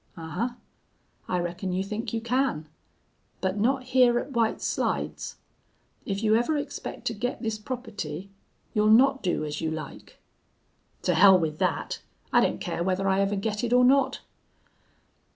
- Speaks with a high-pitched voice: Yes, high, 215 Hz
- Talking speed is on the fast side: No, average, 160 wpm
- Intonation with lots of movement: No, average, 4.9 semitones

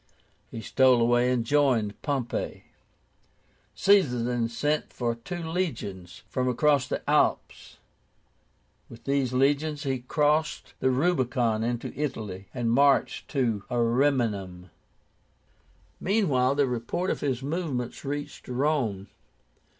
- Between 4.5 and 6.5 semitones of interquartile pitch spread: No, average, 3.9 semitones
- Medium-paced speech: No, slow, 110 wpm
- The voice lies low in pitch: Yes, low, 130 Hz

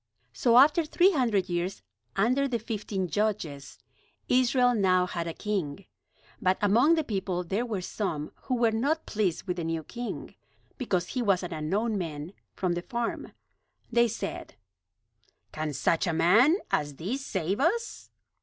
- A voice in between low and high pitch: No, high, 200 Hz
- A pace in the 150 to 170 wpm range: Yes, average, 155 wpm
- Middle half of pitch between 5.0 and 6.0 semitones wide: Yes, wide, 5.6 semitones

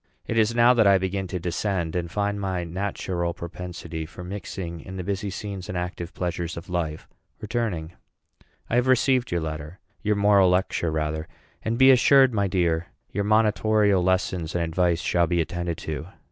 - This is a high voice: No, very low, 90 Hz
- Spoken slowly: No, average, 175 wpm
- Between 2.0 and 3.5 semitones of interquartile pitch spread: Yes, average, 3.2 semitones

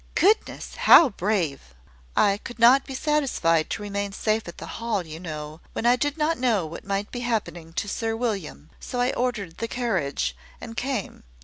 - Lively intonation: Yes, wide, 6.3 semitones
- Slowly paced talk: No, average, 185 wpm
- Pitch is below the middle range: No, high, 215 Hz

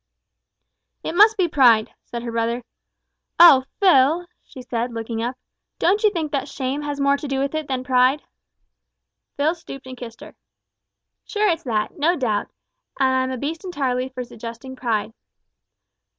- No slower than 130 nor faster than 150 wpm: No, average, 165 wpm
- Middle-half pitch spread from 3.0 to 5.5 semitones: Yes, average, 4.1 semitones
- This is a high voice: Yes, very high, 265 Hz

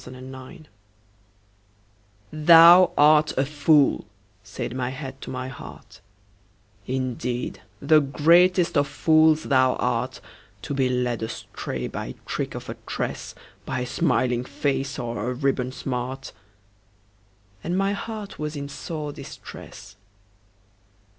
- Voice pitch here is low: Yes, low, 130 Hz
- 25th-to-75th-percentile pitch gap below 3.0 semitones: No, average, 3.8 semitones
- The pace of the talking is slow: Yes, slow, 125 wpm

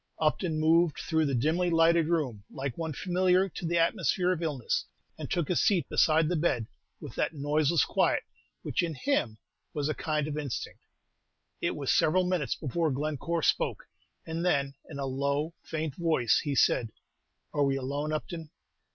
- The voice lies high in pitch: No, medium, 155 Hz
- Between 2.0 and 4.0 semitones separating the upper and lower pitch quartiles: Yes, average, 3.2 semitones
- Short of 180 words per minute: Yes, average, 170 wpm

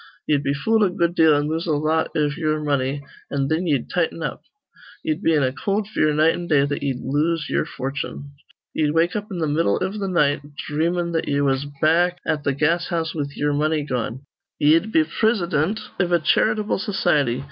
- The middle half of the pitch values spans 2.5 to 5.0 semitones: Yes, average, 3.2 semitones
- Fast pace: Yes, fast, 210 wpm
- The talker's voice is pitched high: No, medium, 155 Hz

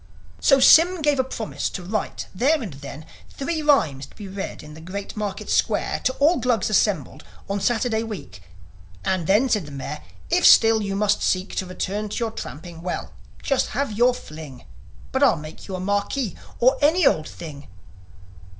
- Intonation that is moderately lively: No, wide, 6.6 semitones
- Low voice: No, high, 205 Hz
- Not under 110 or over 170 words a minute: No, average, 185 wpm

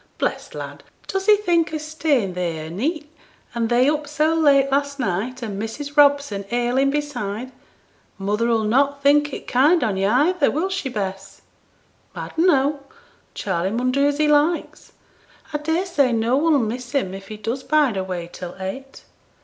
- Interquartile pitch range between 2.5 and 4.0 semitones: No, average, 5.3 semitones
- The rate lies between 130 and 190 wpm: Yes, average, 175 wpm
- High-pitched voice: Yes, very high, 270 Hz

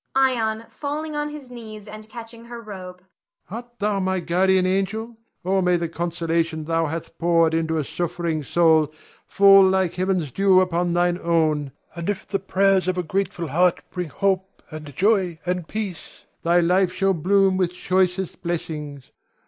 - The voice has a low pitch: No, medium, 185 Hz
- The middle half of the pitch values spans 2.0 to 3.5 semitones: Yes, average, 2.9 semitones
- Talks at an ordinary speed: Yes, average, 165 wpm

